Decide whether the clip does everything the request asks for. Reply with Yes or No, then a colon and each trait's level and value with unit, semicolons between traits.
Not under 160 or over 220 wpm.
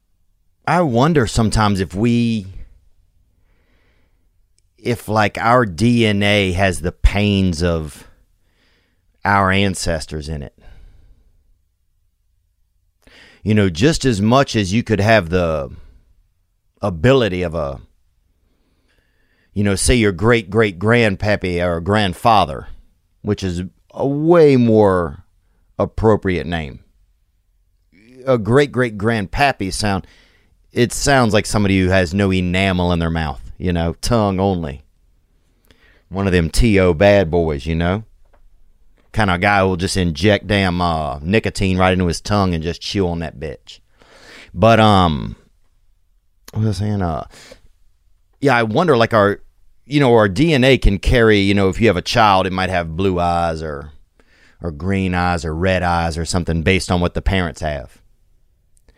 No: average, 140 wpm